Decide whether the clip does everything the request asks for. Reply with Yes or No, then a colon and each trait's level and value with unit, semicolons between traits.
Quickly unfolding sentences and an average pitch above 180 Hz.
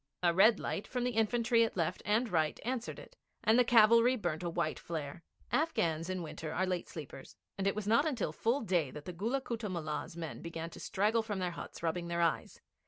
Yes: fast, 220 wpm; high, 190 Hz